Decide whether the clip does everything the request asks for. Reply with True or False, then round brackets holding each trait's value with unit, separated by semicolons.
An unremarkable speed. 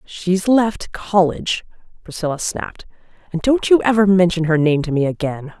True (160 wpm)